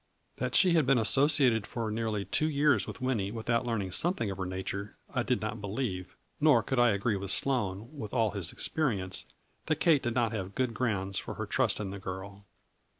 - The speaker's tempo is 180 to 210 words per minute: Yes, fast, 205 wpm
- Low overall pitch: Yes, low, 115 Hz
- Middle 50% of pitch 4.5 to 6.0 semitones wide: Yes, average, 4.8 semitones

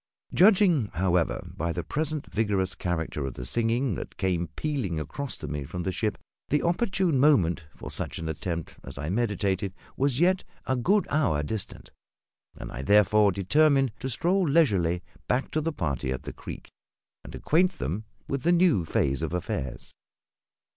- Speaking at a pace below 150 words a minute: No, average, 170 wpm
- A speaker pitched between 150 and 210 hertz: No, low, 105 Hz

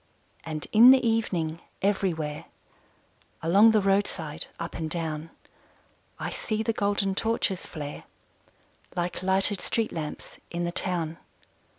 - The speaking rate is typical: No, slow, 120 wpm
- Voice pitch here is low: No, medium, 180 Hz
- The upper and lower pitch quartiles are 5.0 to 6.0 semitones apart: No, average, 4.1 semitones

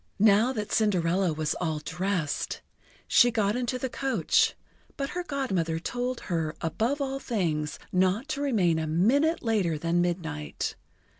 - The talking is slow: No, average, 145 wpm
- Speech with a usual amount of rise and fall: No, wide, 7.0 semitones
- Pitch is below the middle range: No, high, 200 Hz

